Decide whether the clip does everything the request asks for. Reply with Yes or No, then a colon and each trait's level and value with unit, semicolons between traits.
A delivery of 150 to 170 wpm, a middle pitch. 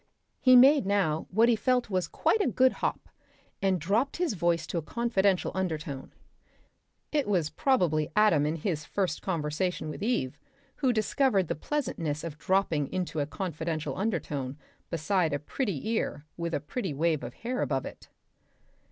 Yes: average, 165 wpm; medium, 180 Hz